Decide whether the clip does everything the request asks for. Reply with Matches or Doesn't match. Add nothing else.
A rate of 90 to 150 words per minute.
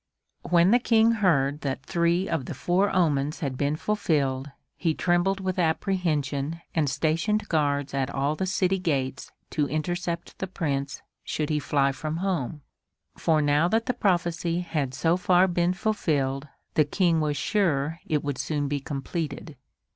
Doesn't match